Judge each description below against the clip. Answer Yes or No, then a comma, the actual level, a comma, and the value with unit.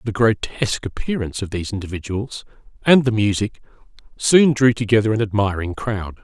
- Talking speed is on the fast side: No, average, 145 wpm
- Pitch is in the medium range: No, low, 110 Hz